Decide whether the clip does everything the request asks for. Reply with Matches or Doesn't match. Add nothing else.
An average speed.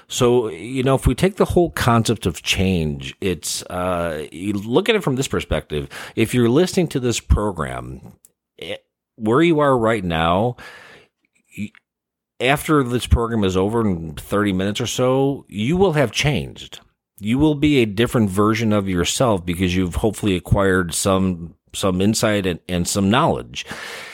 Matches